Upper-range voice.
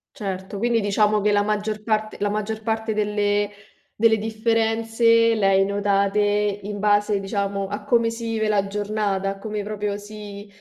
Yes: high, 210 Hz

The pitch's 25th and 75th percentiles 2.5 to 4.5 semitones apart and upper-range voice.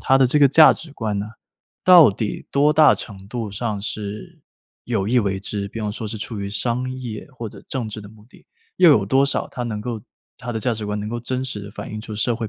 No: average, 3.6 semitones; low, 110 Hz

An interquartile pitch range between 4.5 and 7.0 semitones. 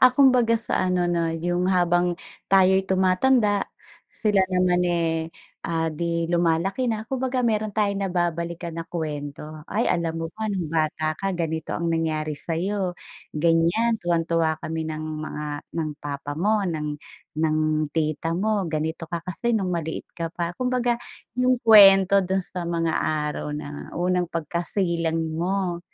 No: average, 3.3 semitones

